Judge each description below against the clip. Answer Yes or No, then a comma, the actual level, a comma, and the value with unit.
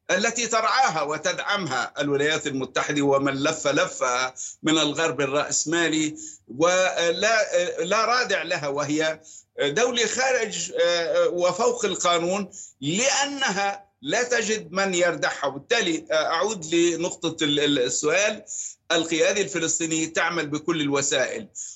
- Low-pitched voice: No, medium, 170 Hz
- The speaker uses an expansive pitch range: Yes, wide, 6.3 semitones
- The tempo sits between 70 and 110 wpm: Yes, average, 95 wpm